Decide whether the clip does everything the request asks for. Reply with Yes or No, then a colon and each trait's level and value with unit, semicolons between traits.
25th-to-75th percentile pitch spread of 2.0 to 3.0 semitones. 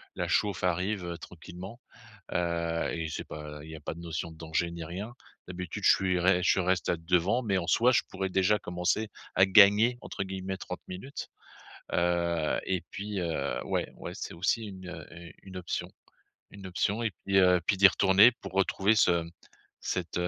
Yes: narrow, 2.4 semitones